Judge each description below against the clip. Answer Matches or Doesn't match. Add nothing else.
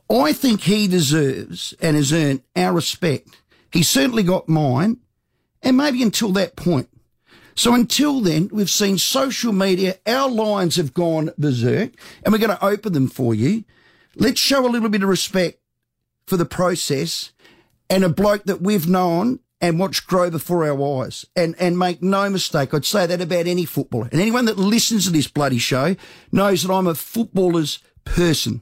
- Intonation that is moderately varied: Matches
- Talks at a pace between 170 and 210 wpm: Matches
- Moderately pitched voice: Matches